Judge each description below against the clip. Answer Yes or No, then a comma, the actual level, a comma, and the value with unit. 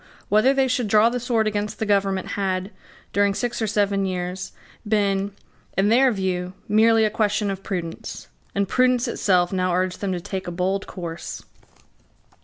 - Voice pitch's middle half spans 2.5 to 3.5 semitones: Yes, average, 2.8 semitones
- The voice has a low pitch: No, high, 200 Hz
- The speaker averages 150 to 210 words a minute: Yes, average, 170 wpm